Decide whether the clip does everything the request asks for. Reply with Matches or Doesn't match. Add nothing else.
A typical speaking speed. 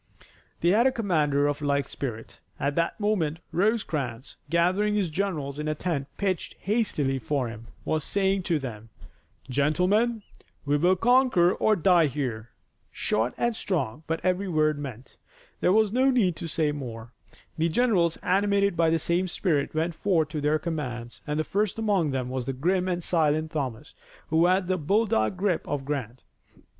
Matches